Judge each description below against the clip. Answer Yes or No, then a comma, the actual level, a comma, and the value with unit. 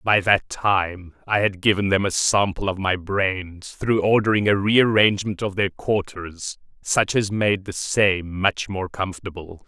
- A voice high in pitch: No, low, 100 Hz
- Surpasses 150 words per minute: Yes, average, 165 wpm